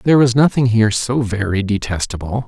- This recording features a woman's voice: No, male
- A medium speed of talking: Yes, average, 170 wpm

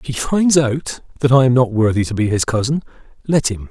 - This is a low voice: Yes, low, 125 Hz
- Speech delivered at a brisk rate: Yes, fast, 245 wpm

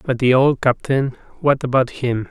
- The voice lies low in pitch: Yes, low, 130 Hz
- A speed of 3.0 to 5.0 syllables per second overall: Yes, 4.5 syllables/s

